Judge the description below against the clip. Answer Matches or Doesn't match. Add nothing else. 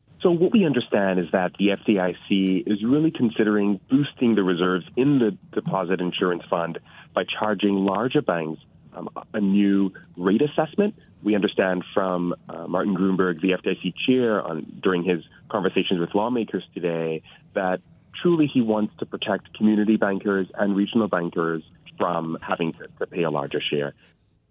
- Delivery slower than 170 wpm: Matches